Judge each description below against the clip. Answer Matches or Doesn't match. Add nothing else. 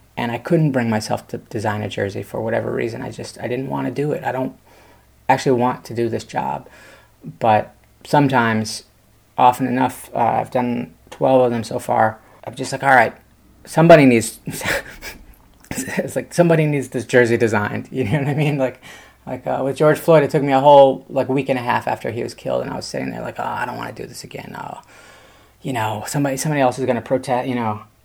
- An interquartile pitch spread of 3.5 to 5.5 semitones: Doesn't match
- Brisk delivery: Matches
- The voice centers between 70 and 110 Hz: Doesn't match